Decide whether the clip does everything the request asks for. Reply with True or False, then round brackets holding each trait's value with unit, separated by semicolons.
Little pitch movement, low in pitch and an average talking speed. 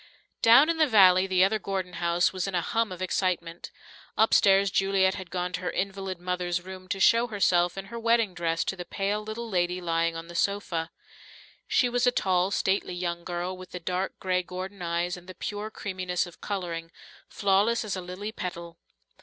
False (2.1 semitones; 185 Hz; 195 wpm)